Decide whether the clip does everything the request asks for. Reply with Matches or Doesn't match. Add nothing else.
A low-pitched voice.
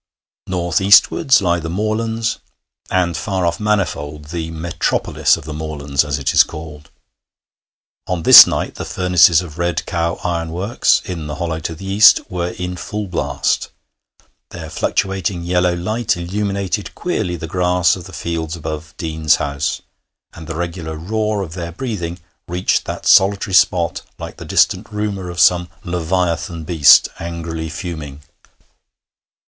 Matches